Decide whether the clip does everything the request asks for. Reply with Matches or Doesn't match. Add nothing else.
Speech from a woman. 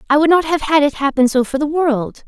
Matches